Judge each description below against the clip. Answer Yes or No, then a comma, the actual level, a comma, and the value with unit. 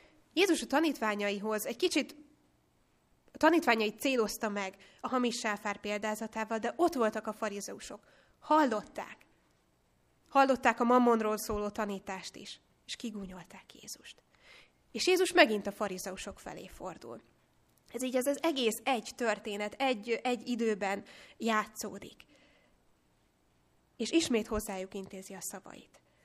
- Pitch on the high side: Yes, high, 220 Hz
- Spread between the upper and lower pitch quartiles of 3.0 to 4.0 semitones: Yes, average, 3.7 semitones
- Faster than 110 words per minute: Yes, average, 120 wpm